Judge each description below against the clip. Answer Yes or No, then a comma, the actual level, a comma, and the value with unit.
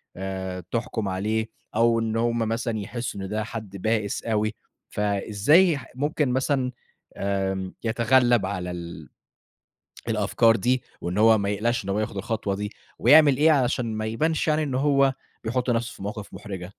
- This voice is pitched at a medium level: No, low, 110 Hz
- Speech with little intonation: No, average, 3.8 semitones